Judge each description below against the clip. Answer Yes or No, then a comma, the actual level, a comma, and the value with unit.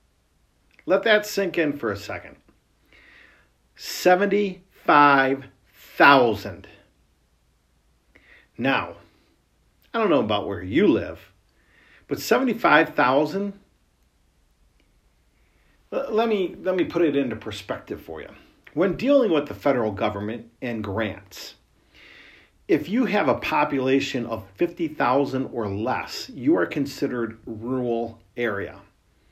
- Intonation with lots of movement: Yes, wide, 8.1 semitones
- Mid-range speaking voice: No, low, 120 Hz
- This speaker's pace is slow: Yes, slow, 100 wpm